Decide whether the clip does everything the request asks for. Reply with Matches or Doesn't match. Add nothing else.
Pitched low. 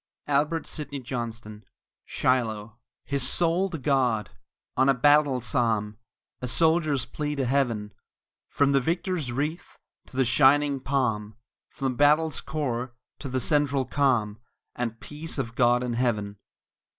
Matches